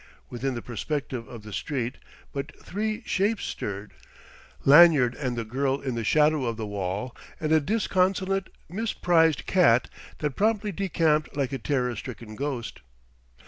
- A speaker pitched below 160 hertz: Yes, medium, 140 Hz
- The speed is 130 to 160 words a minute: Yes, average, 145 wpm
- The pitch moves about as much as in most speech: No, wide, 6.4 semitones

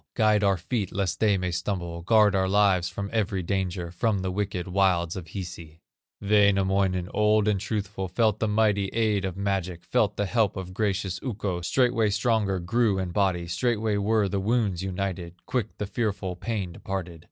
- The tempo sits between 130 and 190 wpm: Yes, average, 175 wpm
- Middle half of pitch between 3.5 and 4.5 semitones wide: No, narrow, 2.5 semitones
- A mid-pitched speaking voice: No, low, 100 Hz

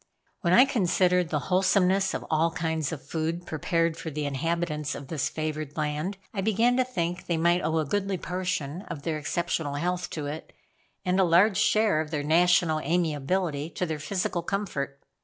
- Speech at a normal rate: Yes, average, 180 wpm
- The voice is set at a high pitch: No, medium, 170 Hz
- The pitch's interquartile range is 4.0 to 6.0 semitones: No, average, 3.1 semitones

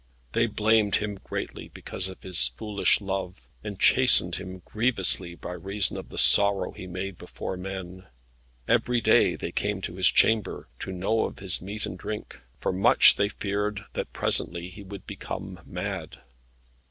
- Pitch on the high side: No, very low, 95 Hz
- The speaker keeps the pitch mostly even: Yes, narrow, 2.2 semitones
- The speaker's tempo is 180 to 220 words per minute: No, average, 165 wpm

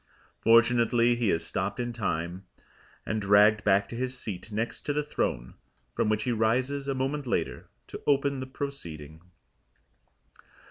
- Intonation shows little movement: No, average, 4.3 semitones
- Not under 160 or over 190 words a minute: No, average, 150 wpm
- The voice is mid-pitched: No, low, 115 Hz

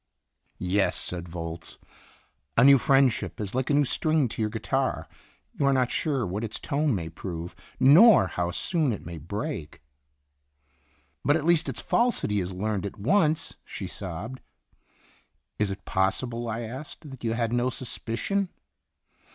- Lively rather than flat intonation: Yes, wide, 6.6 semitones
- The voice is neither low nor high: No, low, 115 Hz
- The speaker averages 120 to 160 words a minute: Yes, average, 155 wpm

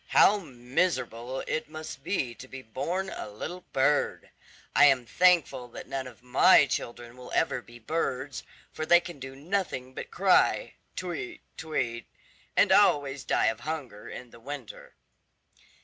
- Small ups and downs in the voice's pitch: No, average, 4.6 semitones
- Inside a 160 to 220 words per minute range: No, average, 150 wpm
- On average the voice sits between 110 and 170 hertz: Yes, low, 135 Hz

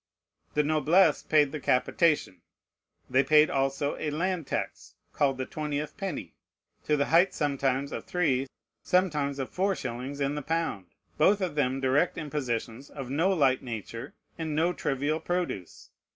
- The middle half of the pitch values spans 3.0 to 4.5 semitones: Yes, average, 3.3 semitones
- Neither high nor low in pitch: Yes, medium, 145 Hz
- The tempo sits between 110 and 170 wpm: Yes, average, 150 wpm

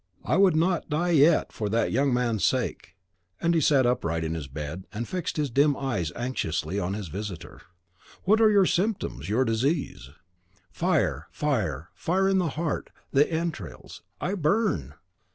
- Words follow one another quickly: No, average, 165 wpm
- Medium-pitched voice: No, low, 130 Hz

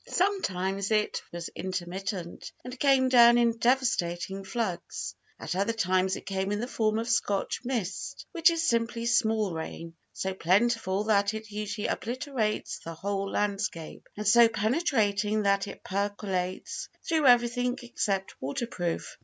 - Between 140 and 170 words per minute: Yes, average, 145 wpm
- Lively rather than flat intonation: No, average, 3.8 semitones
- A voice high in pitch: Yes, high, 210 Hz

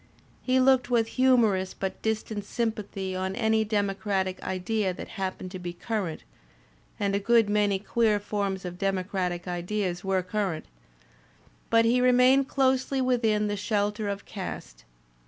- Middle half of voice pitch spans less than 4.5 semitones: Yes, average, 3.2 semitones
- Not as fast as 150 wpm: No, average, 155 wpm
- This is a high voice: Yes, high, 205 Hz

